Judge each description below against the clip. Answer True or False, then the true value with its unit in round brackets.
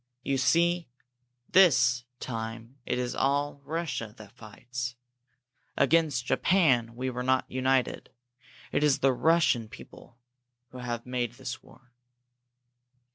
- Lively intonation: False (2.8 semitones)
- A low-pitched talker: True (130 Hz)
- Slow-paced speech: True (120 wpm)